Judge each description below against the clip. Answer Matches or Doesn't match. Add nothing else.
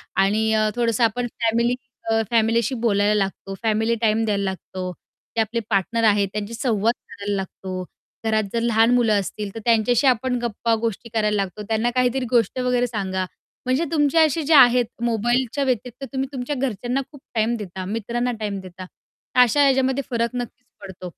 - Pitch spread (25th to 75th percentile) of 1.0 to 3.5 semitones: Matches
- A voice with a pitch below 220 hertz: Doesn't match